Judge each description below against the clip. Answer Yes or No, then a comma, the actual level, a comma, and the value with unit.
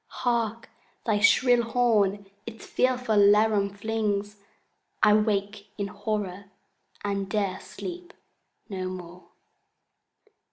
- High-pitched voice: Yes, high, 210 Hz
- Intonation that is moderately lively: No, narrow, 2.1 semitones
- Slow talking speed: Yes, slow, 95 wpm